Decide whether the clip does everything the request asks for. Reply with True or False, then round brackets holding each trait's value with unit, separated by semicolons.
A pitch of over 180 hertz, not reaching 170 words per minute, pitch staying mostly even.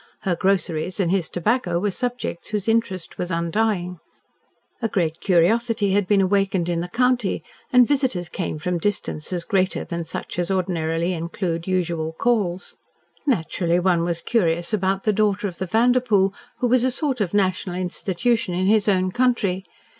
False (190 Hz; 160 wpm; 3.8 semitones)